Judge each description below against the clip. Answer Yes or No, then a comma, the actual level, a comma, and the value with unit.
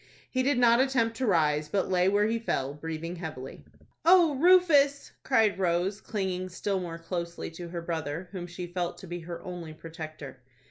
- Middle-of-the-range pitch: Yes, medium, 180 Hz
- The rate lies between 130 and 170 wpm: No, average, 180 wpm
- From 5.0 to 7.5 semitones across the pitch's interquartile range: Yes, wide, 5.4 semitones